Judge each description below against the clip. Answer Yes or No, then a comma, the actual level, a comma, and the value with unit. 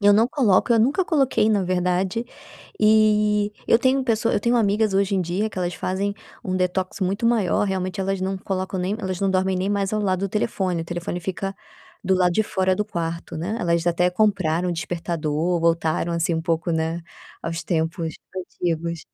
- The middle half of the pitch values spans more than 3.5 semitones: No, average, 3.2 semitones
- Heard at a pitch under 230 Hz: Yes, medium, 185 Hz